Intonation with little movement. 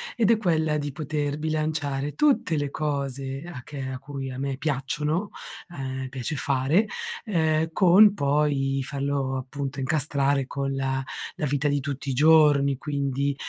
Yes: narrow, 2.3 semitones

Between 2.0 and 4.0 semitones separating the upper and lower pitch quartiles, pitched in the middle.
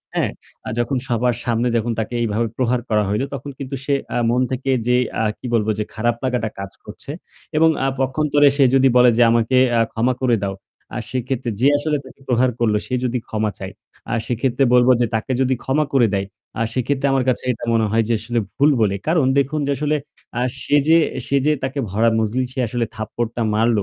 No: average, 2.8 semitones; low, 125 Hz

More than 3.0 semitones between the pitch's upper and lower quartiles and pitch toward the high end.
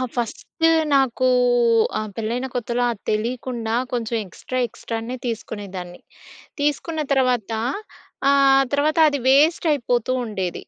Yes: average, 3.6 semitones; high, 245 Hz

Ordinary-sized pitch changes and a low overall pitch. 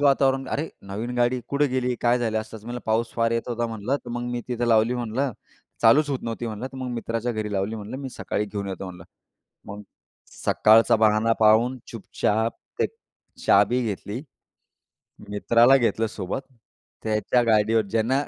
No: narrow, 2.2 semitones; low, 115 Hz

